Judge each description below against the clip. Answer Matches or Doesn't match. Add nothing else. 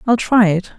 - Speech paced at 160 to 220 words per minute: Doesn't match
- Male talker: Doesn't match